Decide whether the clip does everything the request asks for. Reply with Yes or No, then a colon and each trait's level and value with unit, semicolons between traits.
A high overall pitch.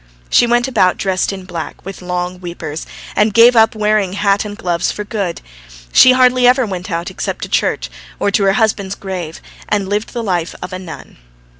Yes: high, 195 Hz